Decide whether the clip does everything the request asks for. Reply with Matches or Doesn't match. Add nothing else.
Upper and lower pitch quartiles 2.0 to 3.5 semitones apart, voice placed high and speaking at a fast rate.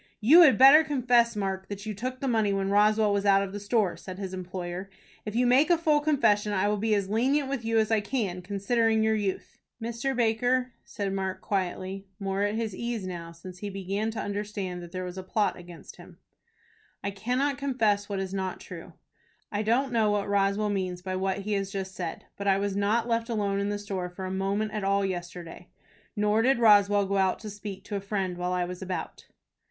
Matches